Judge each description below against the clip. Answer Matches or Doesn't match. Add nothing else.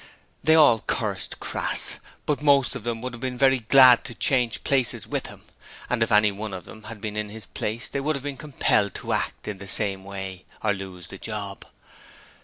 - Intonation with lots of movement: Doesn't match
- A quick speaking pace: Matches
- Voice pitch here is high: Doesn't match